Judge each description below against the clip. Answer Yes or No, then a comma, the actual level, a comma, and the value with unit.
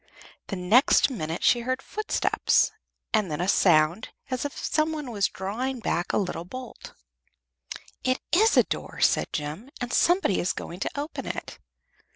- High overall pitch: Yes, high, 230 Hz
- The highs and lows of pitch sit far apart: Yes, wide, 6.8 semitones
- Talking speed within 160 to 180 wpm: Yes, average, 165 wpm